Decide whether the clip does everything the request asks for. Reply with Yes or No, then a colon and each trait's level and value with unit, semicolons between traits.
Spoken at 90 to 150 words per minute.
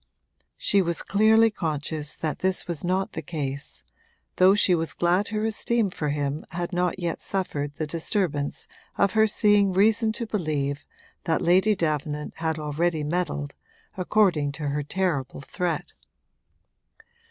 Yes: average, 140 wpm